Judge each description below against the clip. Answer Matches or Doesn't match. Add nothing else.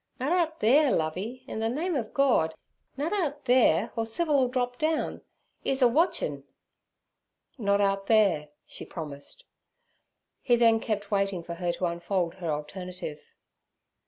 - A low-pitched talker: Doesn't match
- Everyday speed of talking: Matches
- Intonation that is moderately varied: Doesn't match